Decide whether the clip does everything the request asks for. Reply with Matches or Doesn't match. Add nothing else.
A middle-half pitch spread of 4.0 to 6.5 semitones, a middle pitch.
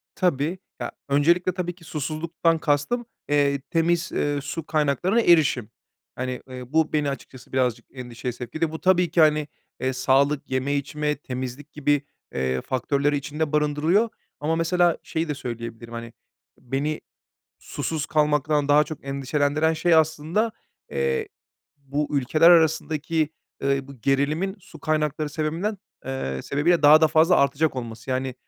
Doesn't match